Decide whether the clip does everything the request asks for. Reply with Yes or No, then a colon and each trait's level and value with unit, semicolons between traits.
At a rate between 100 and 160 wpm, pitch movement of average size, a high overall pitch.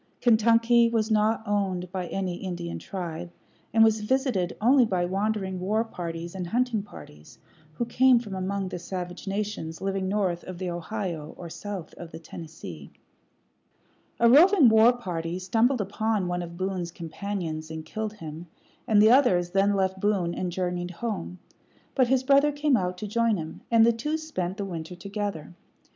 No: average, 170 wpm; average, 4.1 semitones; high, 195 Hz